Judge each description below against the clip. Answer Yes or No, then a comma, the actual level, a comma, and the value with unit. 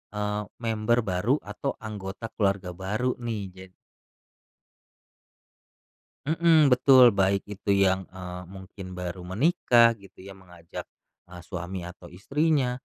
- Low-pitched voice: Yes, low, 100 Hz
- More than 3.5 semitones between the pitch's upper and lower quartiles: Yes, average, 4.1 semitones